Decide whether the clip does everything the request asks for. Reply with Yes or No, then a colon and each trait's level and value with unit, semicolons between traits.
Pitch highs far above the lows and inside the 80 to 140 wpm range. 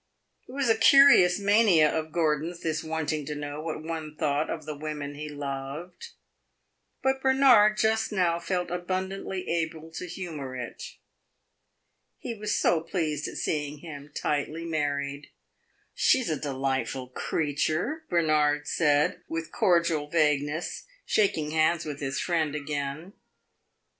No: average, 3.2 semitones; slow, 135 wpm